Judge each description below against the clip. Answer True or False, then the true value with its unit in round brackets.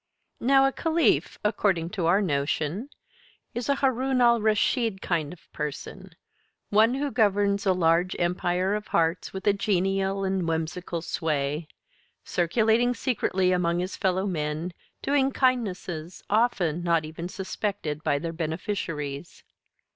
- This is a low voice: False (185 Hz)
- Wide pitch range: False (4.6 semitones)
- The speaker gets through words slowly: True (130 wpm)